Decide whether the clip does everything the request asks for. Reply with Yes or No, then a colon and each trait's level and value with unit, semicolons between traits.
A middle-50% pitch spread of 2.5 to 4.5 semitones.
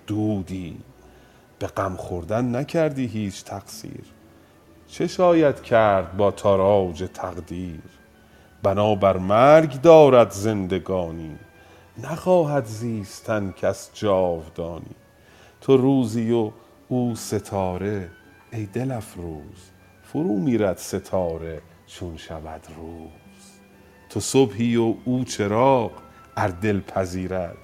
Yes: average, 4.2 semitones